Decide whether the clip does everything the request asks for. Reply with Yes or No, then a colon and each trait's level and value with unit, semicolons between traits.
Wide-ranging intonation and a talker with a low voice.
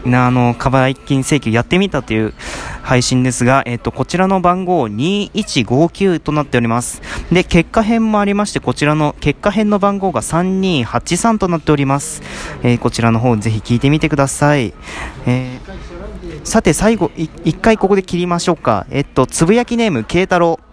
No: wide, 6.7 semitones; medium, 150 Hz